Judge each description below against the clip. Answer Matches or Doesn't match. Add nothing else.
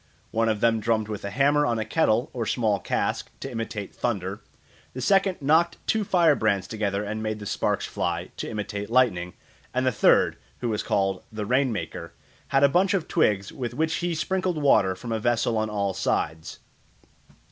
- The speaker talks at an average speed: Matches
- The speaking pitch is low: Matches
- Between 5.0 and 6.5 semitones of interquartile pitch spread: Matches